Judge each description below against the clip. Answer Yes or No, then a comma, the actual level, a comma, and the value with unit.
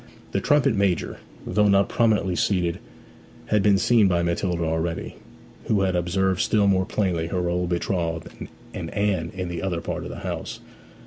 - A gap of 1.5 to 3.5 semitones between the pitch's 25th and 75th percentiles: Yes, narrow, 2.6 semitones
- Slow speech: No, average, 170 wpm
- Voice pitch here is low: Yes, very low, 95 Hz